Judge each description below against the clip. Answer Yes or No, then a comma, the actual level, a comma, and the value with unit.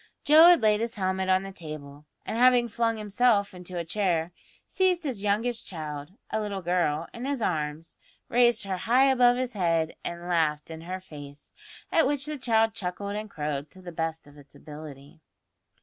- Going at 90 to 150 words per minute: No, average, 185 wpm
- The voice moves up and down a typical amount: No, wide, 6.4 semitones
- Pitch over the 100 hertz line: Yes, high, 190 Hz